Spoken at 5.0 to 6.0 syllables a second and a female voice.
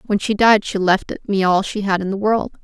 Yes: 5.1 syllables/s; female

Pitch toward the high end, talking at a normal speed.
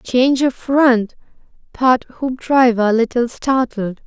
No: high, 245 Hz; slow, 120 wpm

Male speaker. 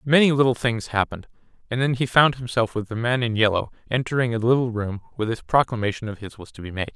Yes: male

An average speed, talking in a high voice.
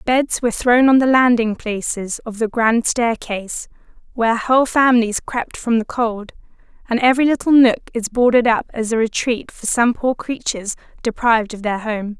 Yes: average, 175 wpm; high, 235 Hz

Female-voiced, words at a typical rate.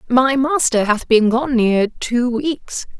Yes: female; average, 160 wpm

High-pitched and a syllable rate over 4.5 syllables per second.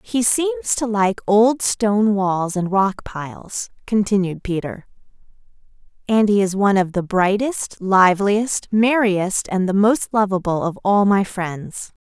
No: high, 200 Hz; 4.0 syllables/s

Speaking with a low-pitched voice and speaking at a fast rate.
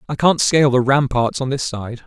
Yes: low, 130 Hz; fast, 230 wpm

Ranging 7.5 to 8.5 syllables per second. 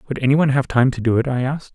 Yes: 7.6 syllables/s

